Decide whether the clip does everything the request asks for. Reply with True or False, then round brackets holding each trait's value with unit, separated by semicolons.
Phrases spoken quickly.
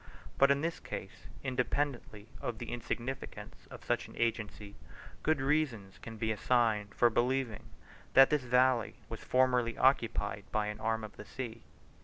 False (155 wpm)